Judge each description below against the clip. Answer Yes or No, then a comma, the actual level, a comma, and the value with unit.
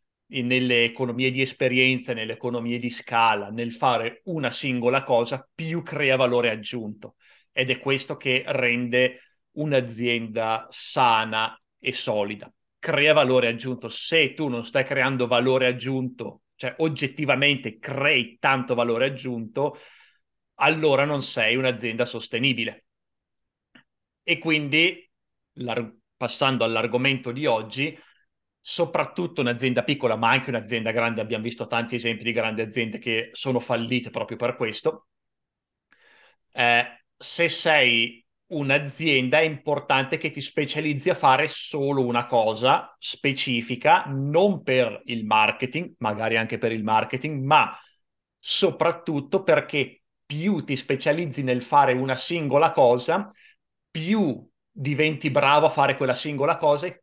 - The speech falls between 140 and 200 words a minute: No, average, 125 wpm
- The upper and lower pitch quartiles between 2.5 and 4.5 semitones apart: Yes, average, 3.7 semitones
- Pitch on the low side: Yes, low, 130 Hz